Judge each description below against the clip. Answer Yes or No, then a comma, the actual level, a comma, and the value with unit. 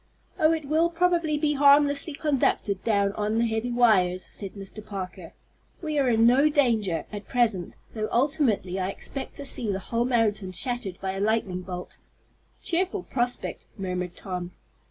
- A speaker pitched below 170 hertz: No, high, 225 Hz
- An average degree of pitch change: No, wide, 6.7 semitones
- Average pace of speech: Yes, average, 160 wpm